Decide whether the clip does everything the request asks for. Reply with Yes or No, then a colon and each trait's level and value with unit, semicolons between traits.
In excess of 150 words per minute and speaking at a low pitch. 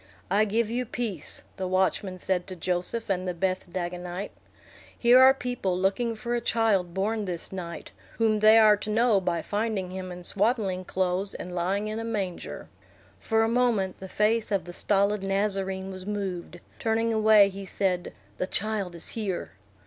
No: average, 175 wpm; high, 195 Hz